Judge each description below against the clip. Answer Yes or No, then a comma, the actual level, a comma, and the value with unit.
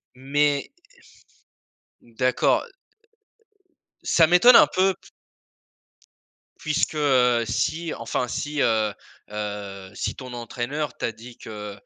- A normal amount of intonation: Yes, average, 4.9 semitones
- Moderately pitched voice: No, low, 125 Hz